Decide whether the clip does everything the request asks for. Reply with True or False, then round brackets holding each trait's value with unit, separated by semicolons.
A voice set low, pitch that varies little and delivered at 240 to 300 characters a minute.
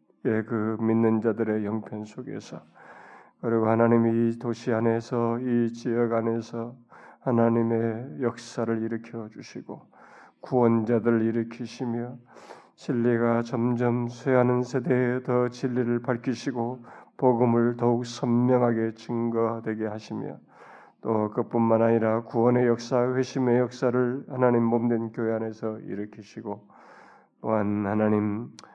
True (115 Hz; 1.4 semitones; 265 characters per minute)